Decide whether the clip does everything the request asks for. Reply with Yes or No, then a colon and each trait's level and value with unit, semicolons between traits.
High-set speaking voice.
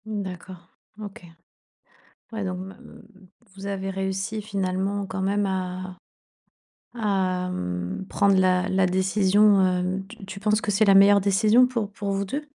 Yes: high, 195 Hz